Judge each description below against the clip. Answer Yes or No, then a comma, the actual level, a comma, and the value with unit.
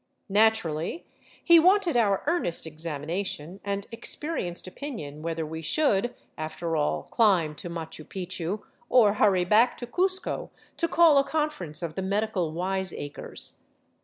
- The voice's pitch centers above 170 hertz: Yes, high, 190 Hz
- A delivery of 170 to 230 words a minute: No, slow, 135 wpm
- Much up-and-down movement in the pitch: Yes, wide, 6.7 semitones